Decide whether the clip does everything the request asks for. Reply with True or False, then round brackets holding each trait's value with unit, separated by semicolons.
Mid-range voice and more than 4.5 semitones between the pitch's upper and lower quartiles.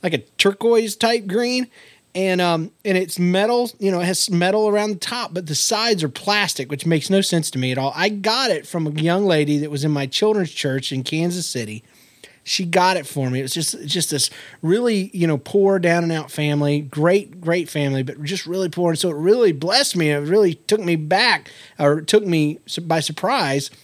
True (175 Hz; 4.9 semitones)